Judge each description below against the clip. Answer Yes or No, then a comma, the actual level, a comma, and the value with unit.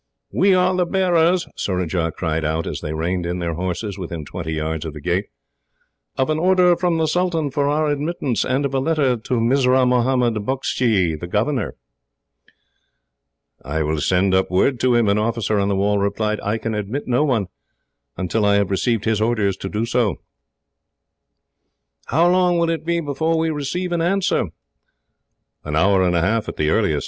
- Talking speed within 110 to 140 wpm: No, average, 185 wpm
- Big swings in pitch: Yes, wide, 8.4 semitones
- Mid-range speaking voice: No, low, 115 Hz